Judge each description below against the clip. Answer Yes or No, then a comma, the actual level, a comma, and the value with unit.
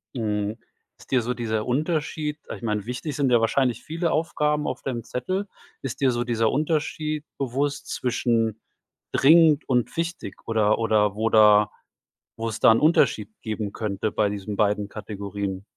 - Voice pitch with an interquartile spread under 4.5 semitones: No, average, 5.3 semitones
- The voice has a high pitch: No, low, 115 Hz